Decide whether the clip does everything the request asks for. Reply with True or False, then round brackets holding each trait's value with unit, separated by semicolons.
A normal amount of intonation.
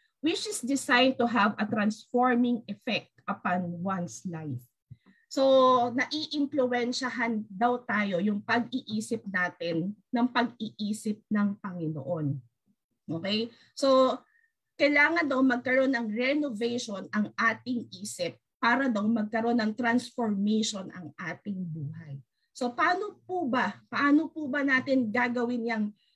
True (4.1 semitones)